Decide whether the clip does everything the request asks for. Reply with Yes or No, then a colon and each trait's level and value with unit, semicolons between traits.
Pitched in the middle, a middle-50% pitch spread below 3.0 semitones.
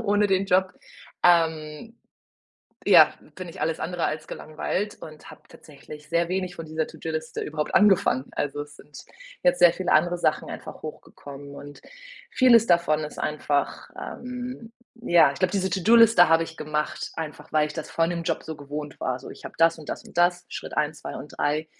No: medium, 165 Hz; average, 3.3 semitones